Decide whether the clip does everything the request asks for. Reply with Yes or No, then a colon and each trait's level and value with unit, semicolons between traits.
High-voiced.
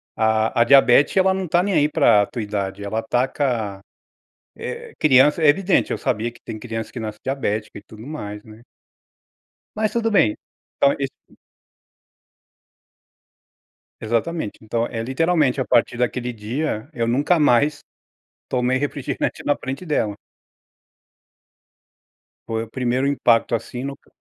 No: low, 125 Hz